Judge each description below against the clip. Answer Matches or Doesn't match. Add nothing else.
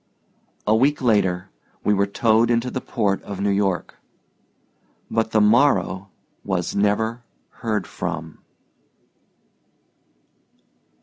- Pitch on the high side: Doesn't match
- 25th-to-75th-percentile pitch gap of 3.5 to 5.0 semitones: Doesn't match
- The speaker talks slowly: Matches